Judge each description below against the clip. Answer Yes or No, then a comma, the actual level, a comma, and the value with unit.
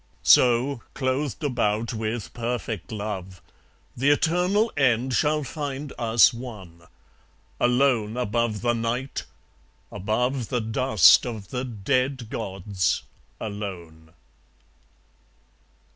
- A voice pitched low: Yes, low, 120 Hz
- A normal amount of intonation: Yes, average, 3.8 semitones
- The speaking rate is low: Yes, slow, 95 wpm